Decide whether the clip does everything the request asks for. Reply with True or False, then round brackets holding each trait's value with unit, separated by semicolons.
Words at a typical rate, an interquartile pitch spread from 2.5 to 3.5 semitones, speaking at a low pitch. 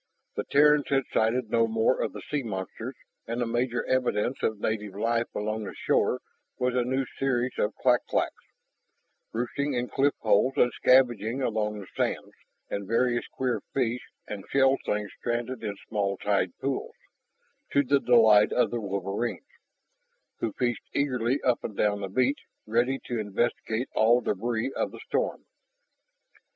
True (160 wpm; 3.2 semitones; 120 Hz)